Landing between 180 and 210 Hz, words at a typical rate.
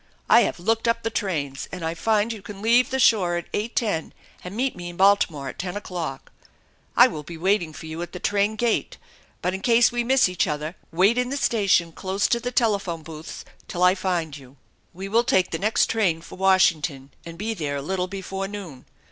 No: high, 190 Hz; fast, 215 wpm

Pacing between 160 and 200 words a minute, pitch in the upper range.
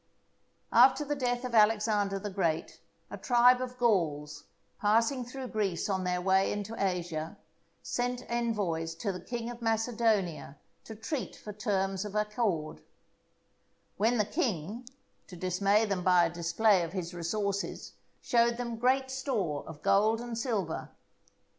No: average, 145 wpm; high, 210 Hz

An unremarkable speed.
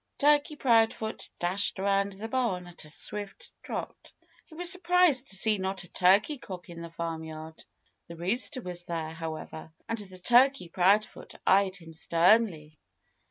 Yes: average, 150 wpm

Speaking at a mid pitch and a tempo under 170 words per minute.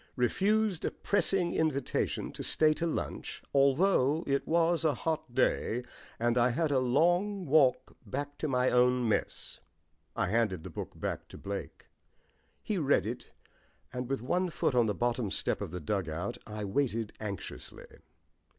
No: low, 130 Hz; average, 160 wpm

